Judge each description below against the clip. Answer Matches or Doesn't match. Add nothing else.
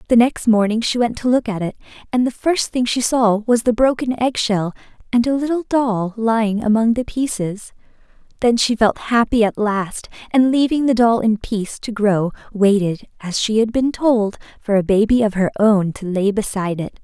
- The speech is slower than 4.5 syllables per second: Doesn't match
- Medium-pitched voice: Doesn't match